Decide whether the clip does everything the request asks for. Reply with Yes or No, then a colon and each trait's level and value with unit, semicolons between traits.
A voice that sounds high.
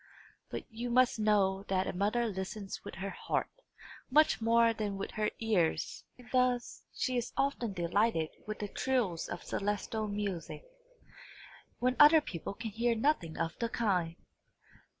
Yes: high, 215 Hz